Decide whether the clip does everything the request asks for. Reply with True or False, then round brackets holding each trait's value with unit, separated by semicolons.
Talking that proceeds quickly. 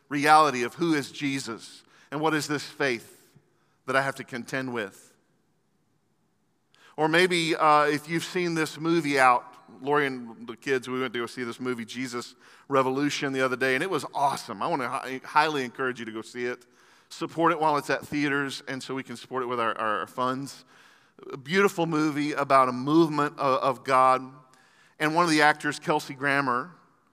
False (195 wpm)